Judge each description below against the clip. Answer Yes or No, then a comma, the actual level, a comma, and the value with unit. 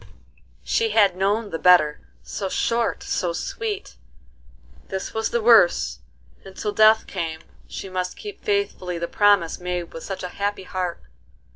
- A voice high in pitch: Yes, high, 195 Hz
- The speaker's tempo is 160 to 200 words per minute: No, average, 150 wpm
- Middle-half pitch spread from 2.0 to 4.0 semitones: Yes, average, 3.6 semitones